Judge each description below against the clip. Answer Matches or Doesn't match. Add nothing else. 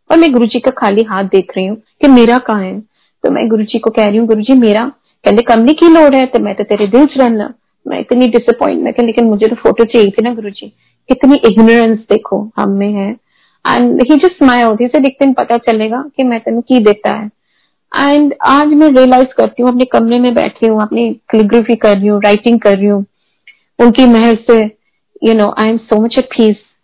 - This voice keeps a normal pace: Doesn't match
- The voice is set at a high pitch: Matches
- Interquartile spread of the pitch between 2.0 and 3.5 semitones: Matches